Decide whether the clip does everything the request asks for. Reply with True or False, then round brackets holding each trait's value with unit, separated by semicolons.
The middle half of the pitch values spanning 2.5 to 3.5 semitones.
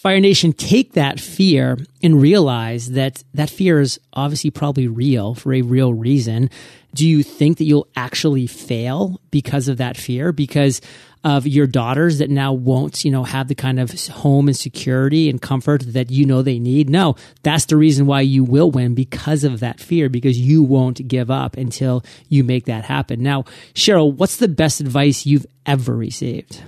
True (2.9 semitones)